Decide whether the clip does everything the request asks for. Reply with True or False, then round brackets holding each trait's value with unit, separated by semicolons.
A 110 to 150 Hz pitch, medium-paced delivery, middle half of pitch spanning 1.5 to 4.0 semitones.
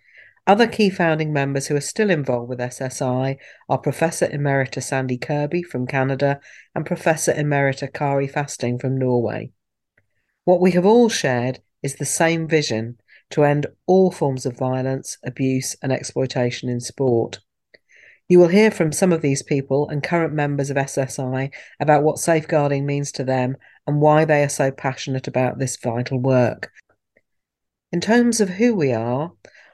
True (140 Hz; 160 wpm; 3.3 semitones)